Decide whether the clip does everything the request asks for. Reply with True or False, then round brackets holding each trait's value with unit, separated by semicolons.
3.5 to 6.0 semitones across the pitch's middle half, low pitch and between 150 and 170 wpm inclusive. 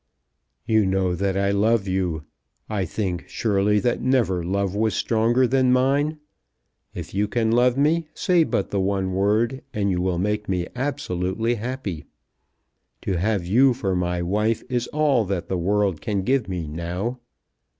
True (4.5 semitones; 105 Hz; 160 wpm)